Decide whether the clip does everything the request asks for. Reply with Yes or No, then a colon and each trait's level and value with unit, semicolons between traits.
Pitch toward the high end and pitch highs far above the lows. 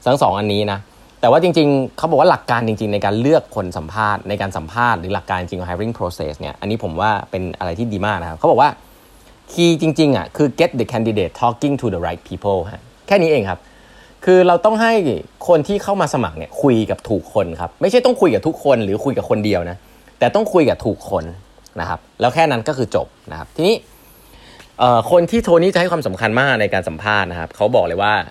No: low, 110 Hz; wide, 8.1 semitones